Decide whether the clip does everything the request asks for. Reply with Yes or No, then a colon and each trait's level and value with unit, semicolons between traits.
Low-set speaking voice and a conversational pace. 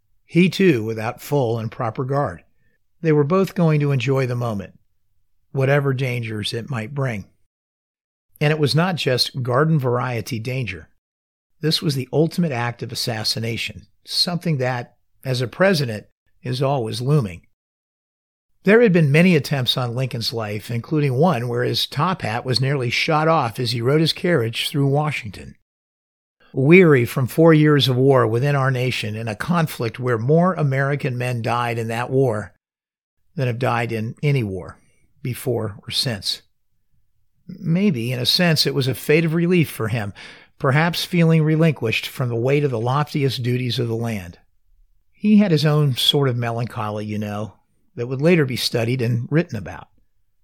Yes: low, 125 Hz; average, 165 wpm